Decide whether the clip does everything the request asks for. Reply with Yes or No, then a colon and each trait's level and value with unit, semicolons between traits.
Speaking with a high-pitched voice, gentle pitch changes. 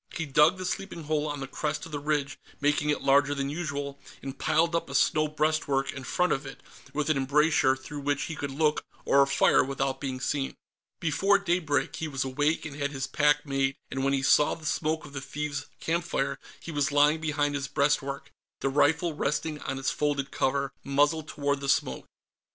No: medium, 145 Hz; narrow, 1.9 semitones